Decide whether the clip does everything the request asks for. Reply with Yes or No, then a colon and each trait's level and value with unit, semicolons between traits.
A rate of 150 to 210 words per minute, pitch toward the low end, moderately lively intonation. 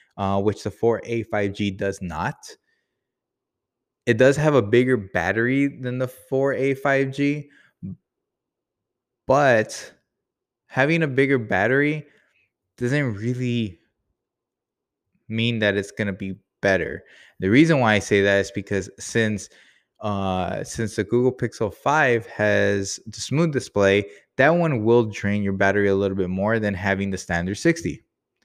No: slow, 135 wpm; low, 110 Hz; average, 4.5 semitones